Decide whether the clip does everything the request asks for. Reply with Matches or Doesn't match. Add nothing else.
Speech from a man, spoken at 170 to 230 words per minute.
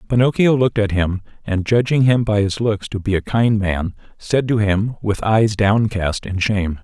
Matches